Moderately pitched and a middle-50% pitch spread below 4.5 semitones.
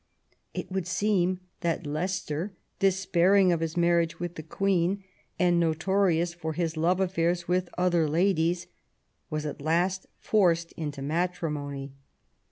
Yes: medium, 175 Hz; narrow, 2.4 semitones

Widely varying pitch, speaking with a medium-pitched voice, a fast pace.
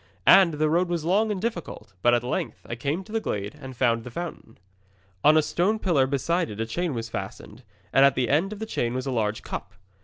Yes: wide, 6.6 semitones; medium, 145 Hz; fast, 240 wpm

